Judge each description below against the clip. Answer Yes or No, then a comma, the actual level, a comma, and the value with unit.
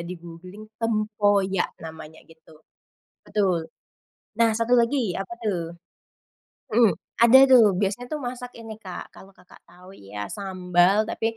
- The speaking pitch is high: Yes, high, 200 Hz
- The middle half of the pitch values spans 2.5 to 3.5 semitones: No, average, 4.0 semitones